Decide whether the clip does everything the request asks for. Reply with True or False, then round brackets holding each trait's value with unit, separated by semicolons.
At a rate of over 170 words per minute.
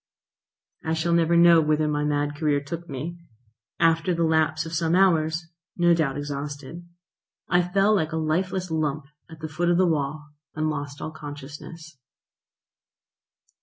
False (155 wpm)